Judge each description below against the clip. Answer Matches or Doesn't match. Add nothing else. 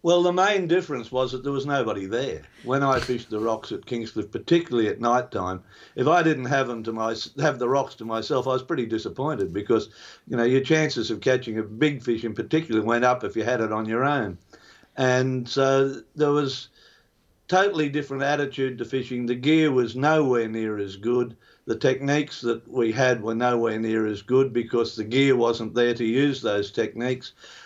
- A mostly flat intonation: Doesn't match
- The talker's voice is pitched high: Doesn't match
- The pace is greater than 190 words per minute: Matches